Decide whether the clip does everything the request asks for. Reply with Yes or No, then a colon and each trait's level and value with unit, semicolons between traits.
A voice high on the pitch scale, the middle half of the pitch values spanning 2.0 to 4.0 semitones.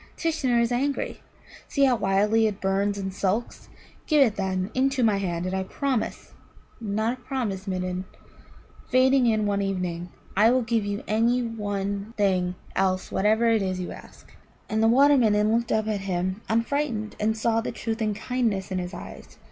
Yes: high, 215 Hz; average, 3.5 semitones